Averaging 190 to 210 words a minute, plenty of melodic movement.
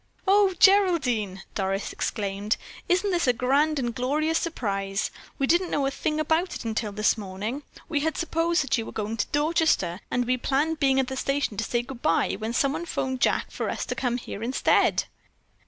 Yes: average, 195 wpm; wide, 6.4 semitones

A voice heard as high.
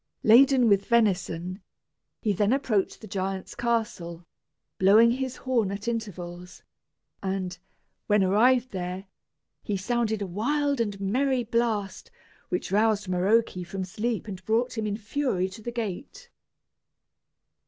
Yes: high, 210 Hz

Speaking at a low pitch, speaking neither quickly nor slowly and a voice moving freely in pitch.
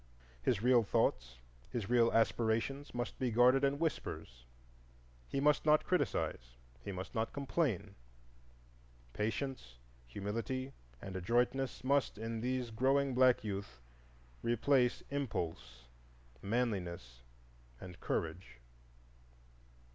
No: low, 115 Hz; slow, 100 wpm; wide, 5.7 semitones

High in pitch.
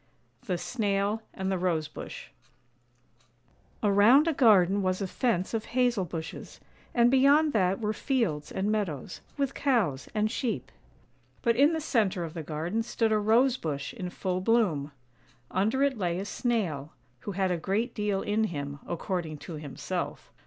Yes: high, 200 Hz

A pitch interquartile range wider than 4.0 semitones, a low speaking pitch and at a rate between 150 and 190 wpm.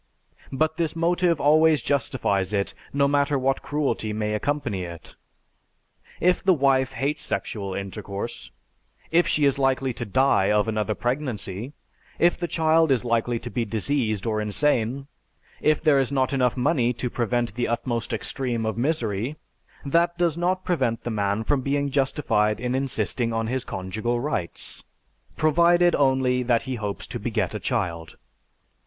Yes: average, 4.8 semitones; low, 130 Hz; average, 155 wpm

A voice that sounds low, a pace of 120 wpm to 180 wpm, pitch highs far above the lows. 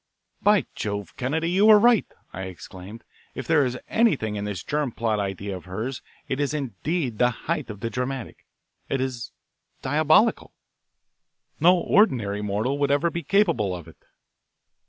Yes: low, 130 Hz; average, 155 wpm; wide, 7.5 semitones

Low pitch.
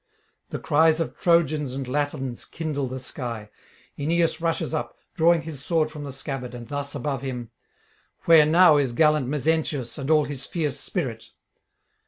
No: medium, 145 Hz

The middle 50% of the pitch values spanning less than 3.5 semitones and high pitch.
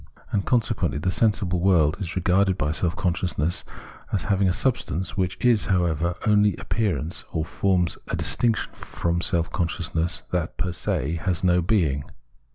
No: average, 2.8 semitones; very low, 90 Hz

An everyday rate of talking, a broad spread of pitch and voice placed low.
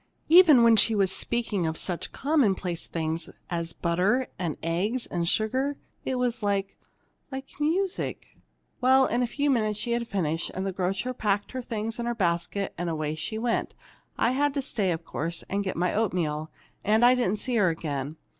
No: average, 185 wpm; wide, 6.0 semitones; high, 210 Hz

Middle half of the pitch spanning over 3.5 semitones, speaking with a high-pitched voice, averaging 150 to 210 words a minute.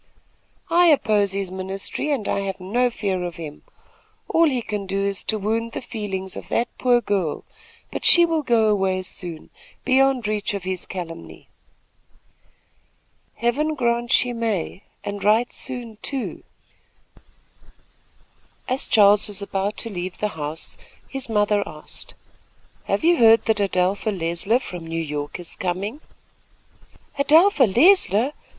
No: average, 4.4 semitones; high, 210 Hz; average, 140 wpm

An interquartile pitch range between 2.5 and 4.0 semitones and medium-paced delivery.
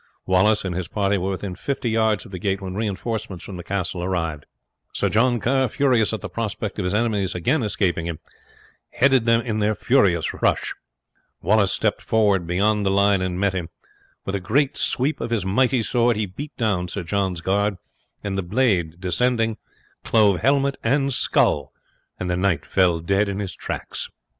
Yes: average, 3.7 semitones; average, 185 wpm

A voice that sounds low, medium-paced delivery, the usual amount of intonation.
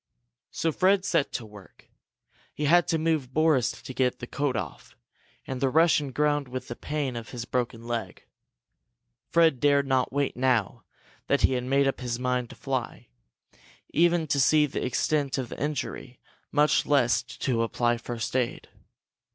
Yes: low, 130 Hz; average, 165 wpm; average, 3.4 semitones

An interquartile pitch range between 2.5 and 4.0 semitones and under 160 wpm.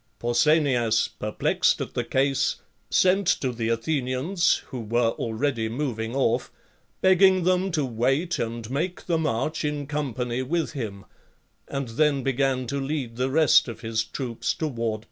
No: average, 4.6 semitones; average, 150 wpm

